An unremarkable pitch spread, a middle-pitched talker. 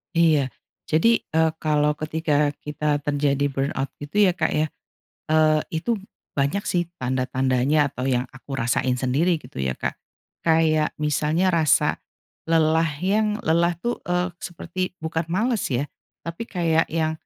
Yes: average, 3.0 semitones; medium, 155 Hz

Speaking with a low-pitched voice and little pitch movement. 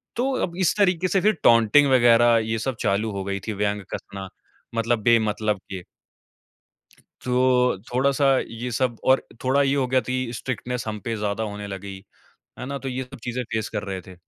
No: low, 120 Hz; average, 3.8 semitones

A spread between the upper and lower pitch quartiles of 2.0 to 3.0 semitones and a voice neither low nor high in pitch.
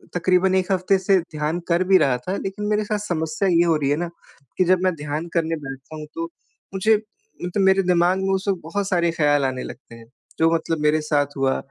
No: average, 3.8 semitones; medium, 170 Hz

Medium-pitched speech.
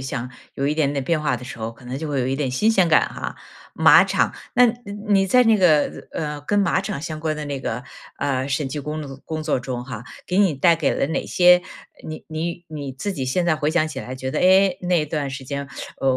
Yes: medium, 150 Hz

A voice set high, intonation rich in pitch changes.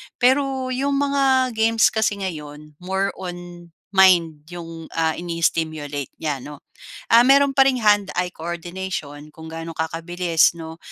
No: medium, 175 Hz; wide, 5.8 semitones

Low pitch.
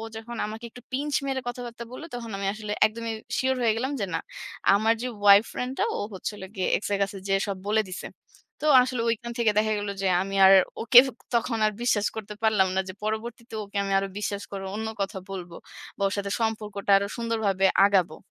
No: high, 215 Hz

